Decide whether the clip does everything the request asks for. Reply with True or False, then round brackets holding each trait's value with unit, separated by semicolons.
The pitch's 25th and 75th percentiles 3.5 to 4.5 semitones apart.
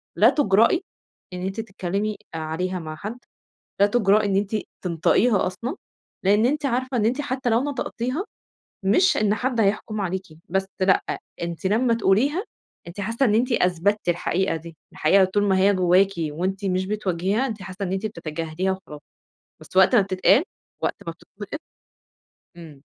True (3.8 semitones)